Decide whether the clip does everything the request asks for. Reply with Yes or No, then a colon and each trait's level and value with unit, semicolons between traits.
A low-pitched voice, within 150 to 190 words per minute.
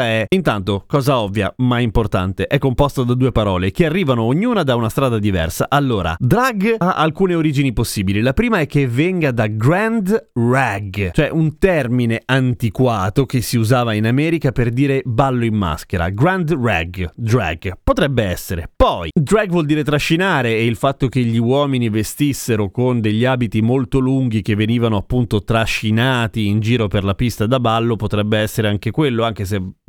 Yes: low, 120 Hz; fast, 170 wpm